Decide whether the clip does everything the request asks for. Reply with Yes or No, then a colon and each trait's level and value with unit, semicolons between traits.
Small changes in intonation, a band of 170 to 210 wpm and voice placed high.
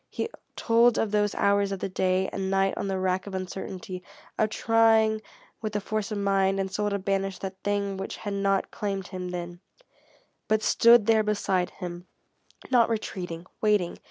Yes: narrow, 2.1 semitones; average, 180 wpm; high, 195 Hz